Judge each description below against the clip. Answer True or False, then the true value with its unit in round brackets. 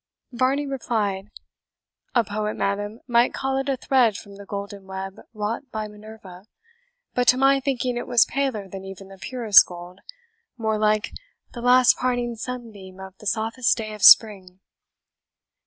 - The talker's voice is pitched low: False (220 Hz)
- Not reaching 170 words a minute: True (155 wpm)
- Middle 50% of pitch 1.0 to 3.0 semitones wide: False (3.8 semitones)